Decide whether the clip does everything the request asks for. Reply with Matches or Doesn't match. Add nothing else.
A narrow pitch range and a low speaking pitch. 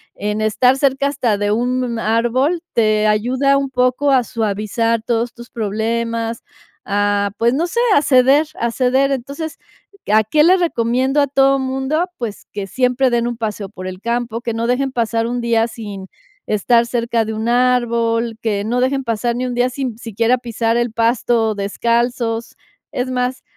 Doesn't match